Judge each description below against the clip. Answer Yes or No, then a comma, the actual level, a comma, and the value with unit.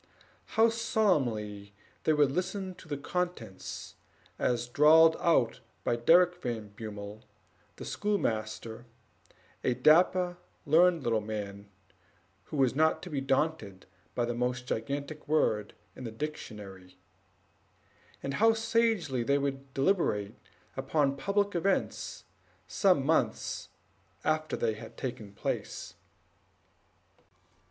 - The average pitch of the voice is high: No, medium, 140 Hz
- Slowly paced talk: Yes, slow, 115 wpm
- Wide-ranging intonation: Yes, wide, 7.4 semitones